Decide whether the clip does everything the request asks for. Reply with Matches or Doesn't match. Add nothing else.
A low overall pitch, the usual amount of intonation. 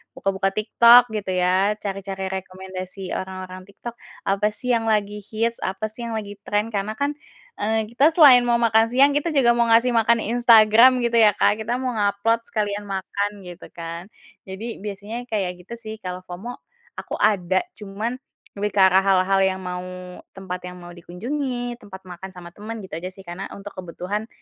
Doesn't match